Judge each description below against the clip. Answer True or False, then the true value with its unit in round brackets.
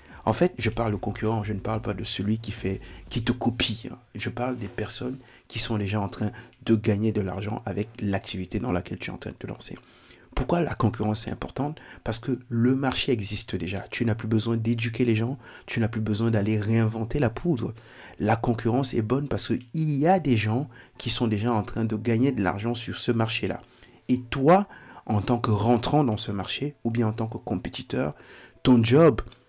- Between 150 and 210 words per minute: False (220 wpm)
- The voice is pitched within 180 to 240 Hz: False (115 Hz)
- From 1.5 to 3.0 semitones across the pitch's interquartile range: True (2.7 semitones)